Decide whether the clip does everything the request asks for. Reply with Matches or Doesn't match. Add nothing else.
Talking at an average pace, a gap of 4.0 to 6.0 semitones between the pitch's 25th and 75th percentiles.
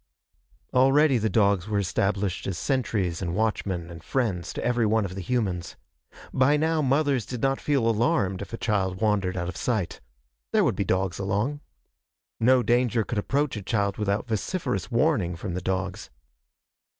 Matches